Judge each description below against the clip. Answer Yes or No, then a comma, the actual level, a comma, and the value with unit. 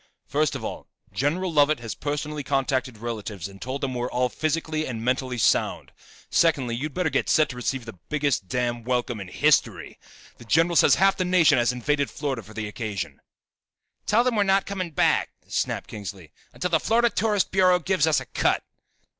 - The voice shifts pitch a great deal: Yes, wide, 5.7 semitones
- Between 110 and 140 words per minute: No, average, 190 wpm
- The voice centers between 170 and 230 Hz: No, medium, 140 Hz